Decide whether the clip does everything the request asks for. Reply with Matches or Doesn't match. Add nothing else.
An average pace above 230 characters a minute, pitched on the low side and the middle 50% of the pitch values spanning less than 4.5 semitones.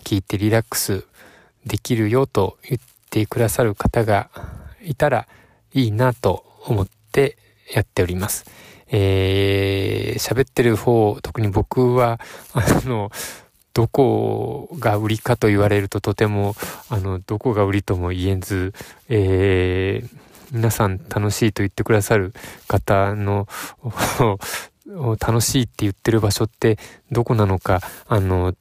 Matches